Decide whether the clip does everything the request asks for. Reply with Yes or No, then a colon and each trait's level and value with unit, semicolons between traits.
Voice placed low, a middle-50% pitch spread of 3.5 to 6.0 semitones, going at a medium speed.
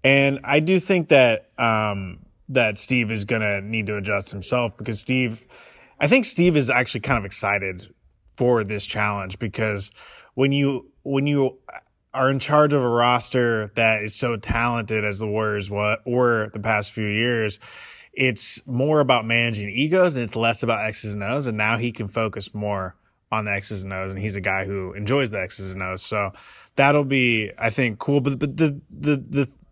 Yes: low, 115 Hz; average, 4.3 semitones; average, 190 wpm